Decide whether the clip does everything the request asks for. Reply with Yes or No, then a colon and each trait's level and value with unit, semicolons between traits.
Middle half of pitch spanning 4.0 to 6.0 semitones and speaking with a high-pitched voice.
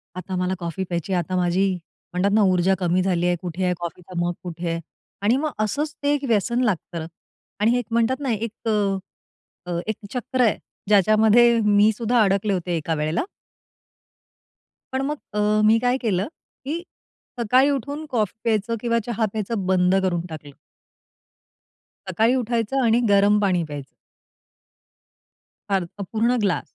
Yes: average, 4.5 semitones; high, 205 Hz